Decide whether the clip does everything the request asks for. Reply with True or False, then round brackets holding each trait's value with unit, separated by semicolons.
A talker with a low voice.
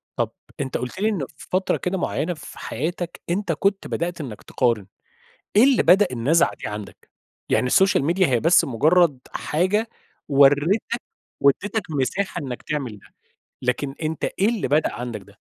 False (155 Hz)